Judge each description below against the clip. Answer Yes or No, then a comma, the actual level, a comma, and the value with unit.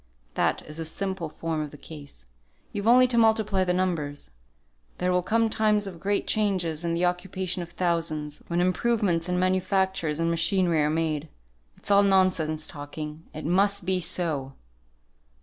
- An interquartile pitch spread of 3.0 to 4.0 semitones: Yes, average, 3.5 semitones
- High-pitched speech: No, medium, 180 Hz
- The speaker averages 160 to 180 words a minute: Yes, average, 165 wpm